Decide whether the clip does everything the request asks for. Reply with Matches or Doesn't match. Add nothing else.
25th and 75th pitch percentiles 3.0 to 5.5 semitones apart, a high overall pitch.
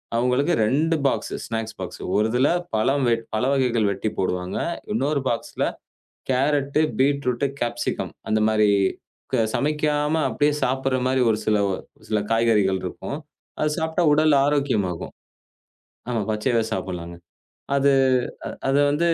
Doesn't match